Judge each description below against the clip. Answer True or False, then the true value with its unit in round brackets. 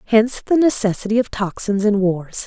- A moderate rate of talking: True (170 wpm)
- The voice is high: True (215 Hz)